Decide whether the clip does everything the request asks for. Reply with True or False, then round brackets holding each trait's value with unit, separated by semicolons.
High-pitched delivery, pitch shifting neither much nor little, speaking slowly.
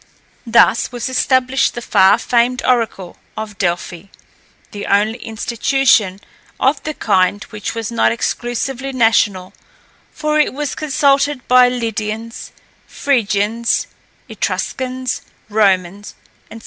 True (230 Hz; 3.8 semitones; 110 wpm)